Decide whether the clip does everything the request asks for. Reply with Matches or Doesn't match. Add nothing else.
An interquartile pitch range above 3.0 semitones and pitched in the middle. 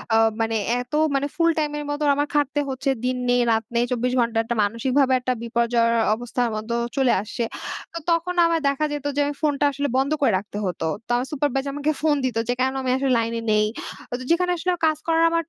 Doesn't match